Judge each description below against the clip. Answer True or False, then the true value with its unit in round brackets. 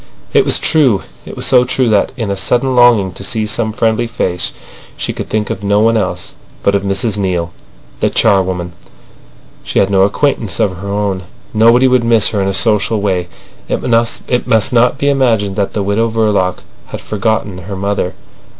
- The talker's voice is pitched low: True (105 Hz)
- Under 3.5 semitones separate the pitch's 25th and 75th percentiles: True (3.0 semitones)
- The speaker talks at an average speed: True (185 wpm)